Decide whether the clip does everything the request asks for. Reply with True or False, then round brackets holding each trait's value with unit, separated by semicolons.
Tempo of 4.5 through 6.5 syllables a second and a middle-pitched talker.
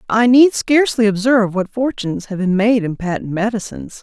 False (5.7 syllables/s; 220 Hz)